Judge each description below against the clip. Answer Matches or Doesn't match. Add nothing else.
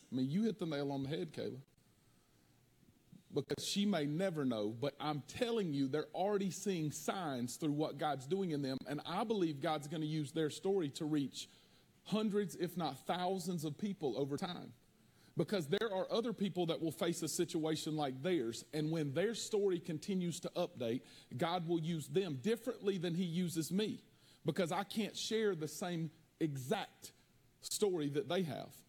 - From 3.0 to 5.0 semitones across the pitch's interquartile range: Matches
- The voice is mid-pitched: Matches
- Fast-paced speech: Doesn't match